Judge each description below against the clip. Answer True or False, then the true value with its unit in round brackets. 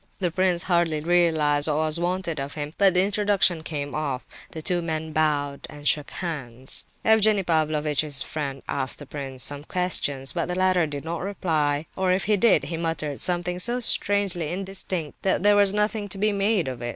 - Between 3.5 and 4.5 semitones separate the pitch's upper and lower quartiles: True (4.2 semitones)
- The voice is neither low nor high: True (165 Hz)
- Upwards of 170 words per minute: True (190 wpm)